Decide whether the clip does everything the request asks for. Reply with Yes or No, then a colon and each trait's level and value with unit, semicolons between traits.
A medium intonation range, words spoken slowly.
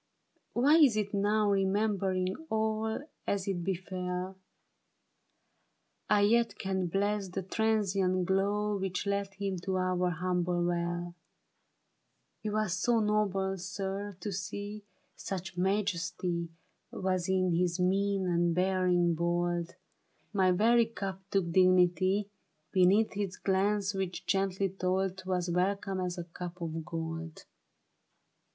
No: narrow, 2.1 semitones; slow, 120 wpm